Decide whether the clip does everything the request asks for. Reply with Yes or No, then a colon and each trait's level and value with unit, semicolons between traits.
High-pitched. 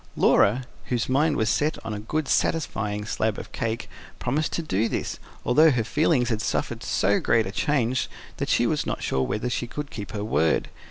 No: low, 115 Hz